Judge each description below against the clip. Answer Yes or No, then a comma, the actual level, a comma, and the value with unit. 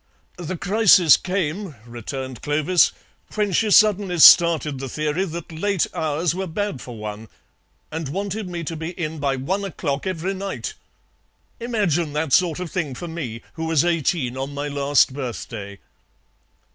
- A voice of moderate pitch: Yes, medium, 160 Hz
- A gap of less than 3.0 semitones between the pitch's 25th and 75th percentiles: No, average, 4.7 semitones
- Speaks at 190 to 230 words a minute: No, average, 155 wpm